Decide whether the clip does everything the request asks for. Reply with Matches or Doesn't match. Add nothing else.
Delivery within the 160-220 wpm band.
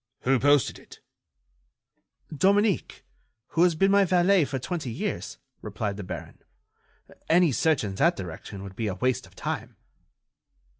Doesn't match